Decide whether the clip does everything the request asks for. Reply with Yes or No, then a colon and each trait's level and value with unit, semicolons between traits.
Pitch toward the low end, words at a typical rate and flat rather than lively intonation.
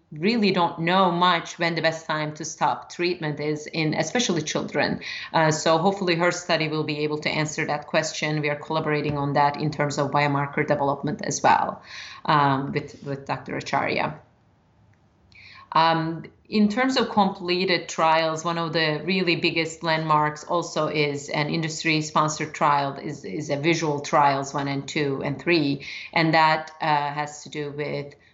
No: medium, 155 Hz; average, 165 wpm; narrow, 2.3 semitones